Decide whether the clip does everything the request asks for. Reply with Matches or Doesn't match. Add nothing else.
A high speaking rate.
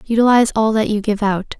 Matches